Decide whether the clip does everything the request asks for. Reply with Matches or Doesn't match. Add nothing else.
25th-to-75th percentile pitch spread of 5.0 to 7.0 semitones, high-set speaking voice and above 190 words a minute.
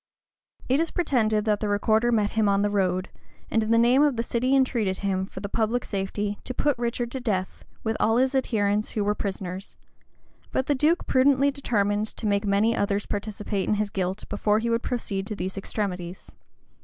Doesn't match